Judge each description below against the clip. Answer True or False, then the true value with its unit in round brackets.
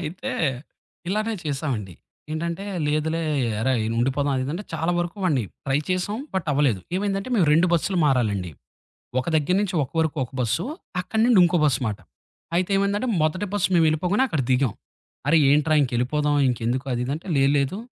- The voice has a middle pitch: True (155 Hz)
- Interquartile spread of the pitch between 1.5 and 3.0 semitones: False (5.4 semitones)